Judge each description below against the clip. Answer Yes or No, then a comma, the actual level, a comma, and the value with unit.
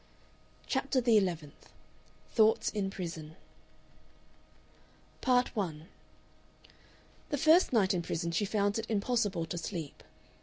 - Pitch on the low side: No, high, 200 Hz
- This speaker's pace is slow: Yes, slow, 110 wpm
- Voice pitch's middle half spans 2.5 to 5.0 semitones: No, wide, 5.5 semitones